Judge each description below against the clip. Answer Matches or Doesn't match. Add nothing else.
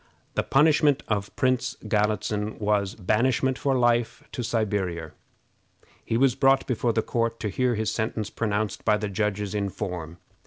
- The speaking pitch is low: Matches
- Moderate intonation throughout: Matches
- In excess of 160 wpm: Doesn't match